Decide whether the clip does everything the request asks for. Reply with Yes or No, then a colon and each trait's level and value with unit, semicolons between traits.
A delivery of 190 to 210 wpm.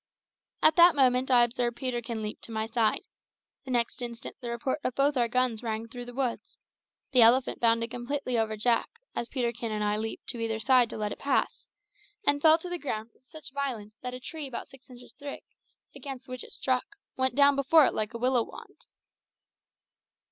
Yes: average, 200 wpm